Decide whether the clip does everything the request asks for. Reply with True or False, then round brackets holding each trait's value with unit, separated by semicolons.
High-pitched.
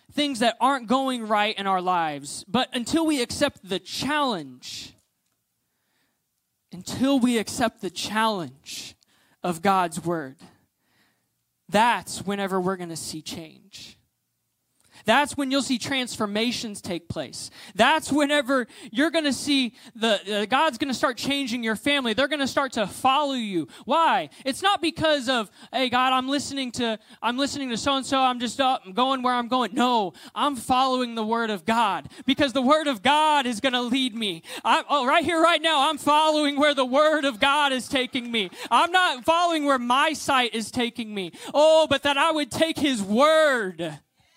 True (260 Hz)